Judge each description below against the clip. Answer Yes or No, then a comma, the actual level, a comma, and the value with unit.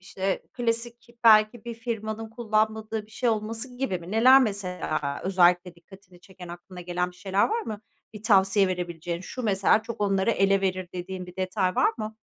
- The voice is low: No, high, 195 Hz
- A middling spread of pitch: Yes, average, 3.5 semitones